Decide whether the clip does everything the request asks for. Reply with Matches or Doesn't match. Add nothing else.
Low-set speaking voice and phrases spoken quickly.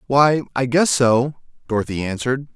Doesn't match